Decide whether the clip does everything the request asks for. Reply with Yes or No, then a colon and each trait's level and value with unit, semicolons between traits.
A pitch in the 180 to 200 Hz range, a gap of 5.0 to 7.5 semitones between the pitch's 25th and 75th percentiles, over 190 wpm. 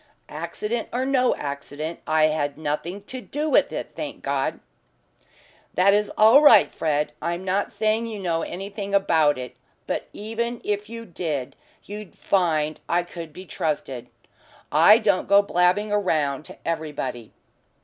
No: medium, 185 Hz; wide, 5.4 semitones; average, 150 wpm